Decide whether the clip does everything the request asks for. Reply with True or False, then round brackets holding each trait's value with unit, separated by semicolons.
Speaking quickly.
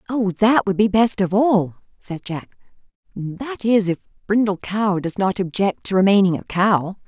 False (180 wpm)